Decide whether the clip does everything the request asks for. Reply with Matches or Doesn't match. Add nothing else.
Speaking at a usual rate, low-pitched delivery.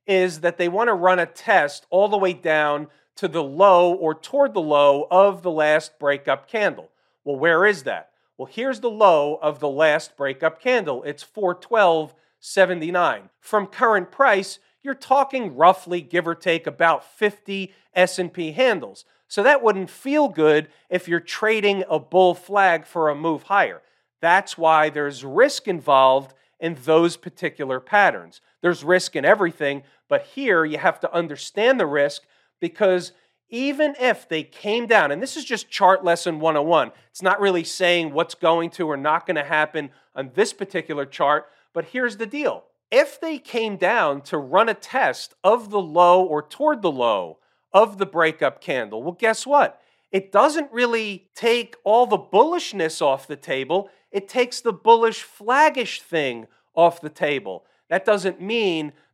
Doesn't match